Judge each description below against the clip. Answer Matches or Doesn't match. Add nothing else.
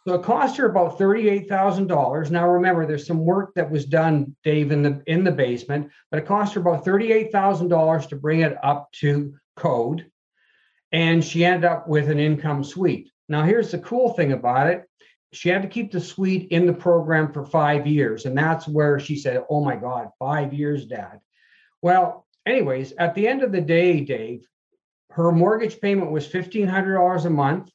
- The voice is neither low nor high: Matches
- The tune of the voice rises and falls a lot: Doesn't match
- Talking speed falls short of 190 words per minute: Doesn't match